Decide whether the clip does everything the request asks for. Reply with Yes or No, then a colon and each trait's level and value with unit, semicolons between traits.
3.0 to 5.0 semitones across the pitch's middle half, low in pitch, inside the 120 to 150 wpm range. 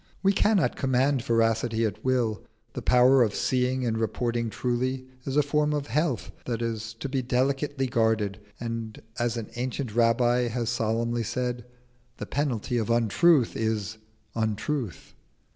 No: narrow, 2.5 semitones; low, 120 Hz; average, 145 wpm